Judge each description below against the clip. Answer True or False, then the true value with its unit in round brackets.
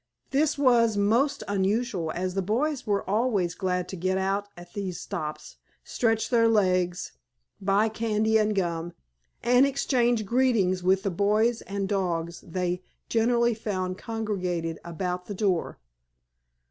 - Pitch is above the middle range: True (200 Hz)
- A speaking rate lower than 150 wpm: True (135 wpm)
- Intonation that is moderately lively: True (3.9 semitones)